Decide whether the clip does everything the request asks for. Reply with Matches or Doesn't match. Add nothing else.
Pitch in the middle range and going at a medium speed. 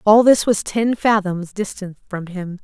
Doesn't match